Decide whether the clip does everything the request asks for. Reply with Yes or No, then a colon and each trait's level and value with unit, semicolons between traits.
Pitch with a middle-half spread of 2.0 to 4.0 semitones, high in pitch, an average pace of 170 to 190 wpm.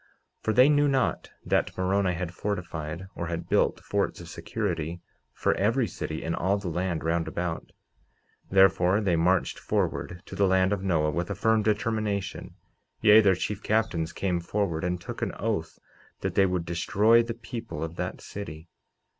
No: average, 3.6 semitones; very low, 95 Hz; average, 175 wpm